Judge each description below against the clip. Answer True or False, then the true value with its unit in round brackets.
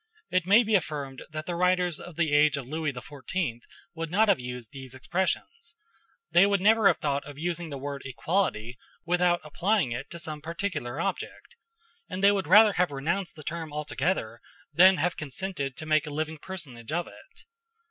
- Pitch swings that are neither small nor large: True (4.6 semitones)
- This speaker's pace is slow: False (185 wpm)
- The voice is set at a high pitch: False (165 Hz)